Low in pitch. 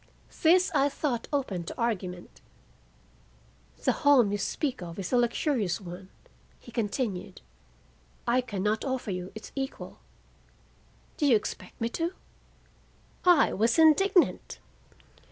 No: high, 235 Hz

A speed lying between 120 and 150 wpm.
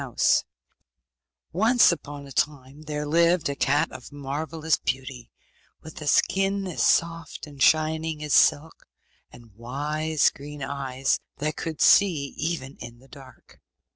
Yes: average, 140 wpm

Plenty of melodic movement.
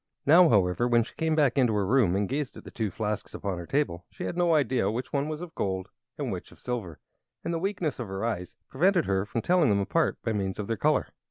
Yes: wide, 7.4 semitones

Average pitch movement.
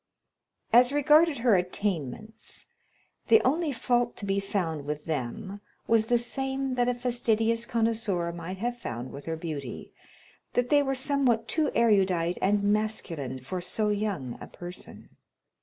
No: wide, 5.8 semitones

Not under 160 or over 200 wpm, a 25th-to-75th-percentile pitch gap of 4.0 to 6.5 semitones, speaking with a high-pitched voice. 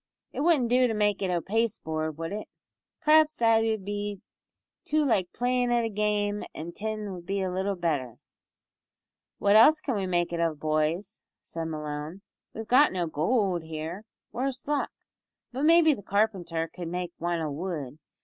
Yes: average, 170 wpm; average, 5.3 semitones; high, 195 Hz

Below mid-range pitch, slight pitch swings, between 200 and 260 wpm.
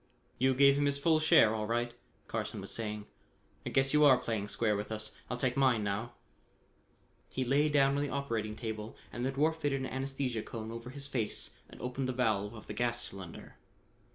No: low, 125 Hz; average, 3.9 semitones; fast, 205 wpm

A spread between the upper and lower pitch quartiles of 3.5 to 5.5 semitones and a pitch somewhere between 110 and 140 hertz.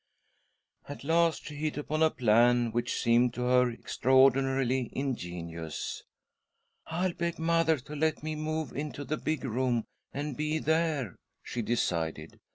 Yes: average, 4.5 semitones; low, 135 Hz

